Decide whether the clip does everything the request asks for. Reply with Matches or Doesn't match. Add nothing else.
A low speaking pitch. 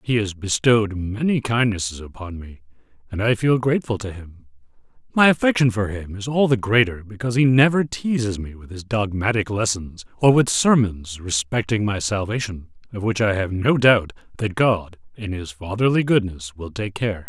Matches